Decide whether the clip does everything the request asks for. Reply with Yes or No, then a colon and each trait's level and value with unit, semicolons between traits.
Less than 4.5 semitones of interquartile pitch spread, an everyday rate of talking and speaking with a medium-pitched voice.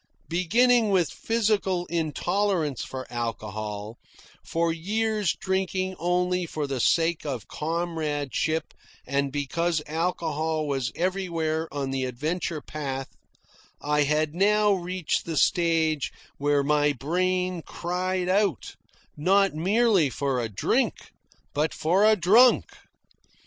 No: average, 4.1 semitones; slow, 115 wpm; medium, 165 Hz